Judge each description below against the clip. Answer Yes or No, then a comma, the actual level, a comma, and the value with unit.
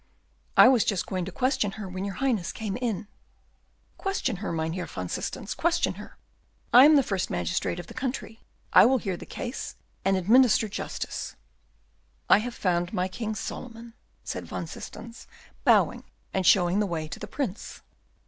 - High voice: Yes, high, 205 Hz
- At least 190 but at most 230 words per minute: No, average, 170 wpm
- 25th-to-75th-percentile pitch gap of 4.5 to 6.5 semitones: Yes, average, 5.0 semitones